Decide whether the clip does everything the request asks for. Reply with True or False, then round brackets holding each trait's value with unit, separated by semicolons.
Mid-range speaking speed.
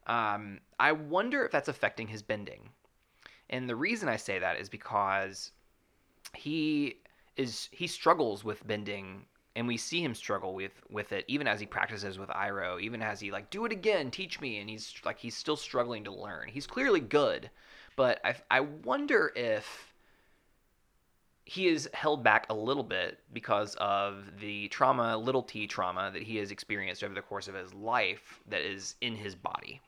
True (180 wpm)